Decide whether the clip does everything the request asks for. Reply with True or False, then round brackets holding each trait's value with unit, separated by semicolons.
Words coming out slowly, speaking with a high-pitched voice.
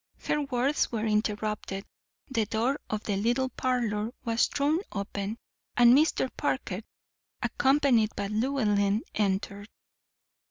True (115 wpm; 225 Hz)